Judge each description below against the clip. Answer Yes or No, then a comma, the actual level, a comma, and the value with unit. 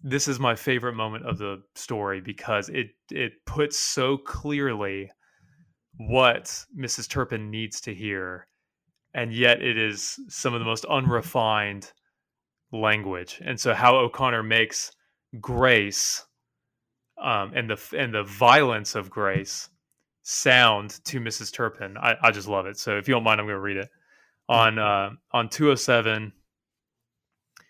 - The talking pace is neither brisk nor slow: Yes, average, 145 wpm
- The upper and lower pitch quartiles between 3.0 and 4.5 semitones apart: Yes, average, 3.8 semitones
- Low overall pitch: Yes, low, 115 Hz